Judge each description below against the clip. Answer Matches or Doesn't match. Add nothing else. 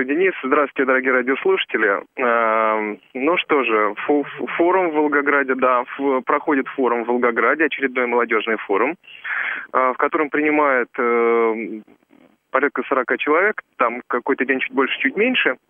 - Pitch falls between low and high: Doesn't match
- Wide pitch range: Doesn't match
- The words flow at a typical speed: Matches